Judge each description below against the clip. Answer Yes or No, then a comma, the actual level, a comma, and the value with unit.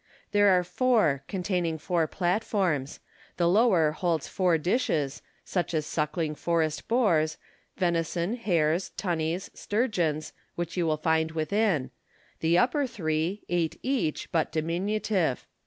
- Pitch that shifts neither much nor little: Yes, average, 3.9 semitones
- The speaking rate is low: Yes, slow, 125 wpm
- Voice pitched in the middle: Yes, medium, 170 Hz